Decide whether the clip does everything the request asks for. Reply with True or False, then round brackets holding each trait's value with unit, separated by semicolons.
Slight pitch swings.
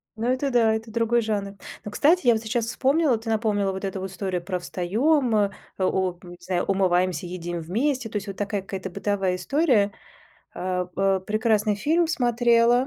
False (4.1 semitones)